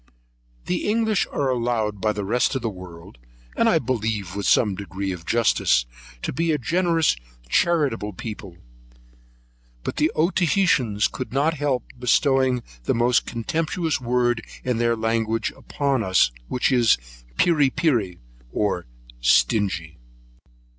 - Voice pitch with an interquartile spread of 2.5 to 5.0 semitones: No, wide, 5.6 semitones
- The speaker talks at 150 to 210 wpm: No, slow, 135 wpm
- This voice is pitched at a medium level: No, low, 120 Hz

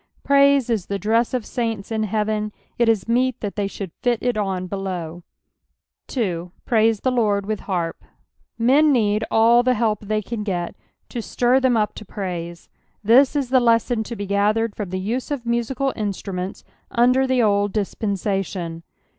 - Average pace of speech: Yes, average, 170 wpm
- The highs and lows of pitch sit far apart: No, average, 3.4 semitones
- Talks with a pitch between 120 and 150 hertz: No, high, 215 Hz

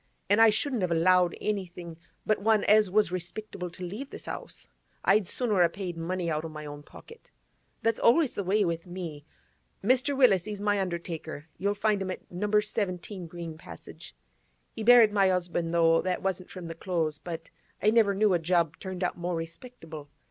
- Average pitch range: Yes, average, 3.7 semitones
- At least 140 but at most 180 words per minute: No, average, 190 wpm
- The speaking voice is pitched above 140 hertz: Yes, medium, 185 Hz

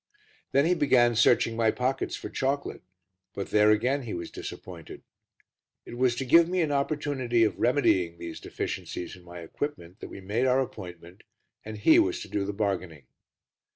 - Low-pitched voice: Yes, low, 120 Hz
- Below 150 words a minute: No, average, 175 wpm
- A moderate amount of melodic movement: No, wide, 6.4 semitones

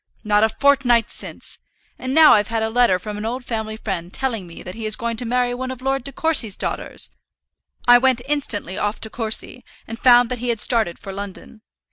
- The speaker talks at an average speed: No, fast, 215 wpm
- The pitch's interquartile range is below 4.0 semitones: Yes, average, 2.9 semitones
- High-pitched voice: Yes, high, 230 Hz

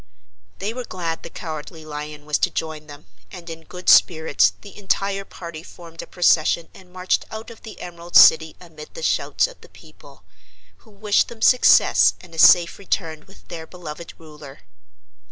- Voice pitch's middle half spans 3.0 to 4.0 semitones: Yes, average, 3.6 semitones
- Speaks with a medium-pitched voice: Yes, medium, 170 Hz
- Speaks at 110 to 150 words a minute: No, average, 175 wpm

